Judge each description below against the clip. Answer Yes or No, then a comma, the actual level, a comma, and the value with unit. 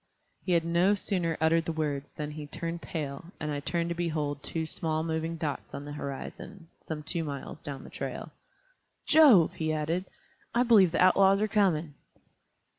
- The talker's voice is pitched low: No, medium, 165 Hz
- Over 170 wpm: Yes, average, 180 wpm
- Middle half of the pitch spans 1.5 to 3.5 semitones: Yes, average, 2.7 semitones